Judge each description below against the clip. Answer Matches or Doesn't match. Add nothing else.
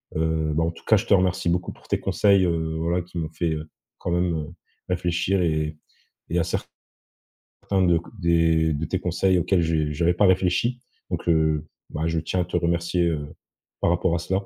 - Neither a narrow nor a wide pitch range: Doesn't match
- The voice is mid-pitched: Doesn't match